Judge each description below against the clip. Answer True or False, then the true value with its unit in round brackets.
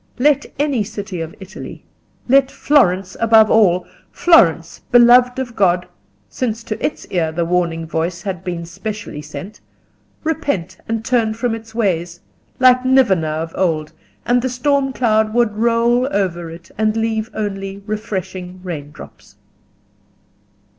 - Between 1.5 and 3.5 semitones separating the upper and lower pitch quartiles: False (5.3 semitones)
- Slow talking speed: True (130 wpm)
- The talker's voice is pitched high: True (215 Hz)